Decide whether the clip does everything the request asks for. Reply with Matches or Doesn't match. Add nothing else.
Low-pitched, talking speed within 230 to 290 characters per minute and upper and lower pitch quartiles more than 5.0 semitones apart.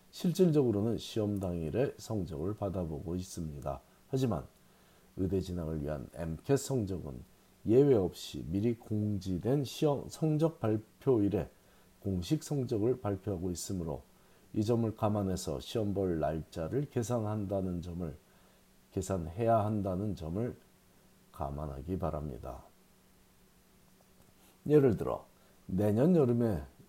Matches